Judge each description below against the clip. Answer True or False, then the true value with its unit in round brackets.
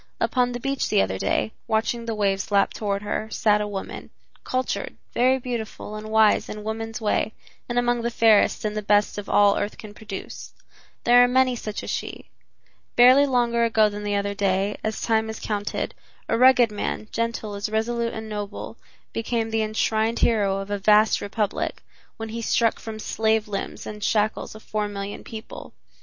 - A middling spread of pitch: False (2.0 semitones)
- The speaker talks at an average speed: True (185 wpm)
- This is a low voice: False (220 Hz)